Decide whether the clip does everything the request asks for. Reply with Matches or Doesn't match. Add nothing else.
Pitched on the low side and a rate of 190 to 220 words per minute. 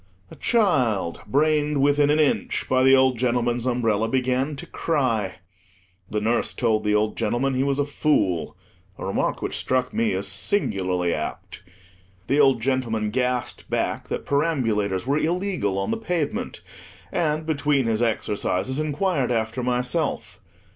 Doesn't match